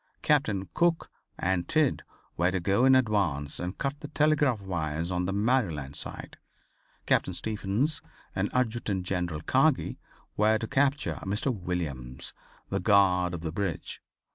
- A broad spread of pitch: Yes, wide, 6.5 semitones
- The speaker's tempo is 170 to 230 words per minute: No, average, 140 wpm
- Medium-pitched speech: No, low, 100 Hz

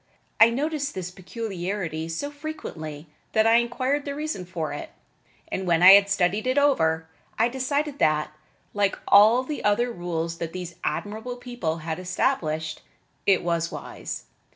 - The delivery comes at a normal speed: Yes, average, 155 wpm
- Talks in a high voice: Yes, high, 200 Hz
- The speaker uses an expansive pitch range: Yes, wide, 6.9 semitones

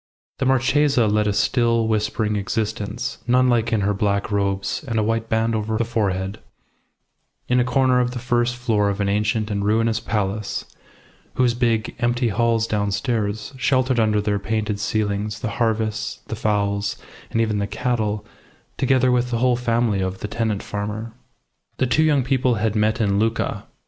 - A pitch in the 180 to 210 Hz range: No, low, 110 Hz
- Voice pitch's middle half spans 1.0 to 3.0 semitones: Yes, narrow, 2.6 semitones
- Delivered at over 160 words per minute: Yes, average, 170 wpm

